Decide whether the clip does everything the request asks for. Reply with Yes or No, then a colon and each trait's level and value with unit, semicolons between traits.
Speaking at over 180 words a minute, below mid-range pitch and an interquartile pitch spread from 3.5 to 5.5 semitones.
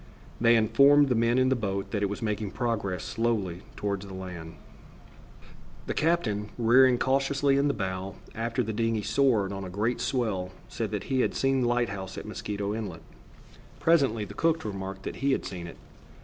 Yes: average, 190 wpm; low, 110 Hz; average, 4.7 semitones